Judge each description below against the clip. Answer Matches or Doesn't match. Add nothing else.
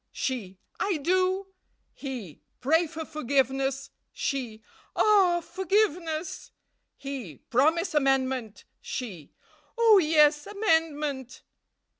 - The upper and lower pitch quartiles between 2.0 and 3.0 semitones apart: Doesn't match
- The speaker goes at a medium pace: Doesn't match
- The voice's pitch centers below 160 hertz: Doesn't match